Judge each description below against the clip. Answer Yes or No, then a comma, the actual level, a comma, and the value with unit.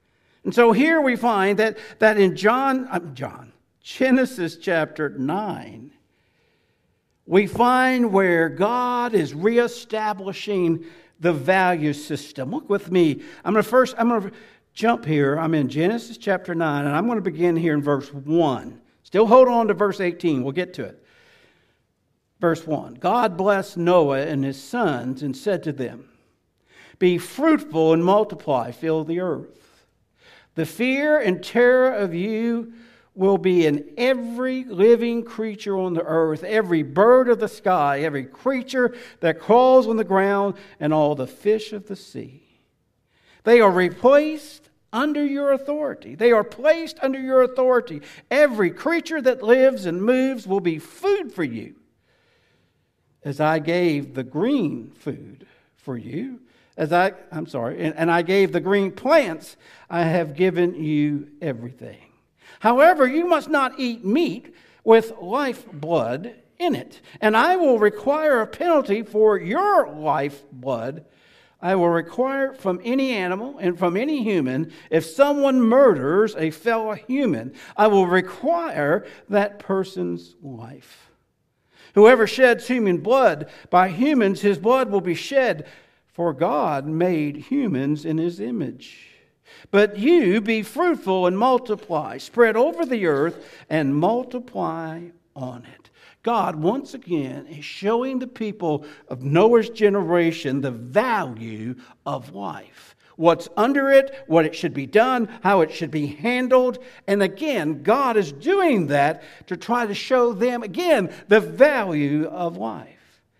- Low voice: No, high, 200 Hz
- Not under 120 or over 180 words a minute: Yes, average, 145 wpm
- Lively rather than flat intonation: Yes, wide, 7.0 semitones